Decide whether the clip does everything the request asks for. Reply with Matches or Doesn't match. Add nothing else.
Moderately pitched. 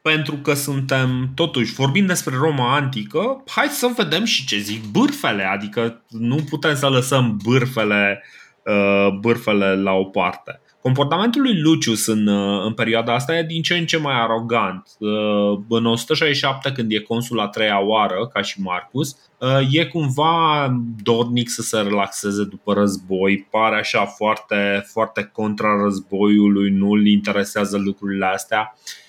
Doesn't match